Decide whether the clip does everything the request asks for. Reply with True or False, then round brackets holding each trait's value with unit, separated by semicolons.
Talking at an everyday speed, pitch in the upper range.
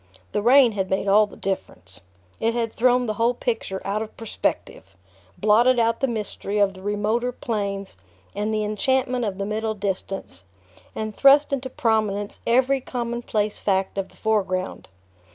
True (160 wpm; 215 Hz)